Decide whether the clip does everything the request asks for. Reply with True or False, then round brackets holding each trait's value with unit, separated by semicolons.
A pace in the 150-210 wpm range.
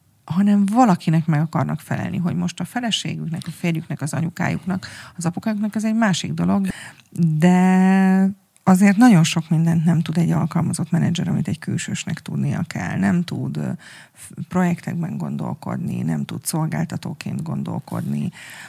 False (135 wpm)